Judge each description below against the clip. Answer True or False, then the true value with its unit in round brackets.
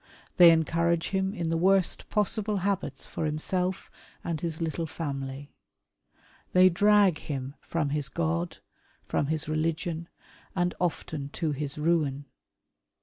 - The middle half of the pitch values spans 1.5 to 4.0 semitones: True (3.5 semitones)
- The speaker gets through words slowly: True (130 wpm)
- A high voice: False (165 Hz)